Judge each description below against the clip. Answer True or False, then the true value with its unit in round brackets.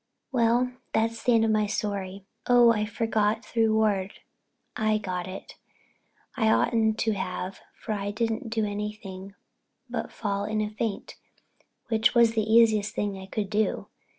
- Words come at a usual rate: True (150 wpm)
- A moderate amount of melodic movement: False (1.9 semitones)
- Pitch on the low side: False (215 Hz)